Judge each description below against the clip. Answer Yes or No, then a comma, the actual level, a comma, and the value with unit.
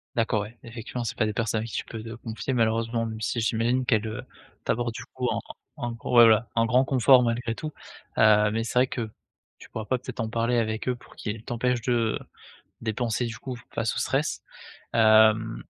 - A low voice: Yes, low, 115 Hz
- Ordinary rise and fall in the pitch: No, narrow, 1.6 semitones